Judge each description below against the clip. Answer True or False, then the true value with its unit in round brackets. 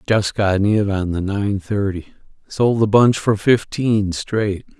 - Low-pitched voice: True (105 Hz)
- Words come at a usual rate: True (165 wpm)